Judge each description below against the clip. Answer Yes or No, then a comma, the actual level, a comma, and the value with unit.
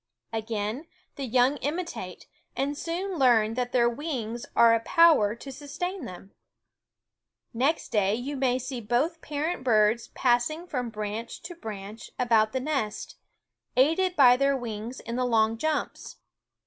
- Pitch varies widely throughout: No, average, 4.5 semitones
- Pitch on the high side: Yes, very high, 250 Hz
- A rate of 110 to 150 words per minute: Yes, average, 145 wpm